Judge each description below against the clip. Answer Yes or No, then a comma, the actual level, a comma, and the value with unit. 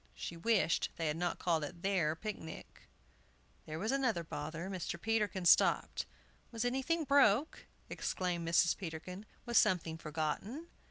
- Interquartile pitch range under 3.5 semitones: No, average, 5.3 semitones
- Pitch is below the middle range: No, medium, 180 Hz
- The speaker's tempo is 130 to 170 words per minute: Yes, average, 140 wpm